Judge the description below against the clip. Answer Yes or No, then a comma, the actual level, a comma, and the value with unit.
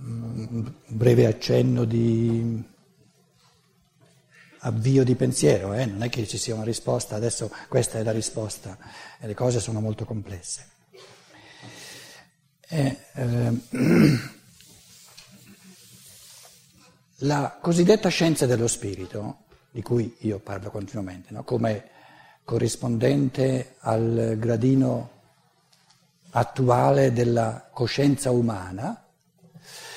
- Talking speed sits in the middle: No, slow, 95 wpm